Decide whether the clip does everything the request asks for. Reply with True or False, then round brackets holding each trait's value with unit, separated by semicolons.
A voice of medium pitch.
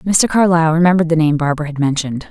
True (160 Hz)